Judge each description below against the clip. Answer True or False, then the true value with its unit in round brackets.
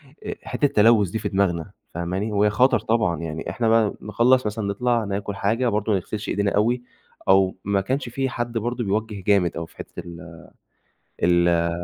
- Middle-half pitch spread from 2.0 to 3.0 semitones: False (3.6 semitones)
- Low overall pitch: True (105 Hz)